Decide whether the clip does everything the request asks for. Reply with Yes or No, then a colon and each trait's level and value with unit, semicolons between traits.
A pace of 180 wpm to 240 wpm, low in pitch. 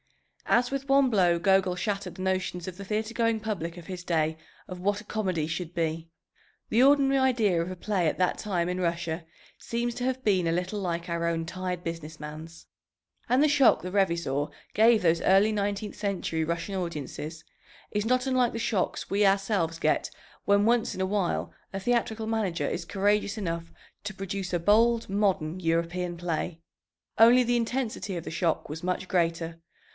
No: average, 185 wpm; high, 190 Hz